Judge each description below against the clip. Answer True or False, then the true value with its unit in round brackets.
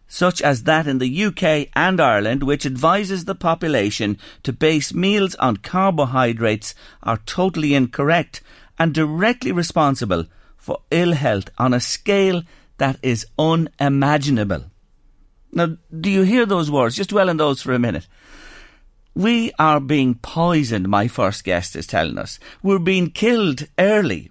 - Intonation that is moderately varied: False (5.9 semitones)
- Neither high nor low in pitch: True (155 Hz)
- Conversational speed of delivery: True (145 wpm)